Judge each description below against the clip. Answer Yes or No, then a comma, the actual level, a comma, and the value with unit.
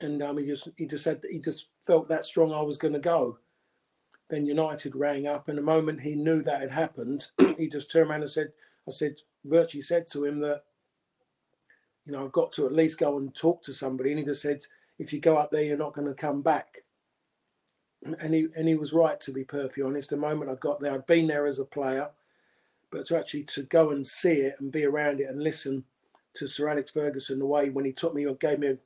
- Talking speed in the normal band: No, fast, 240 wpm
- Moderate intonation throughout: No, narrow, 2.1 semitones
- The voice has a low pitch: No, medium, 145 Hz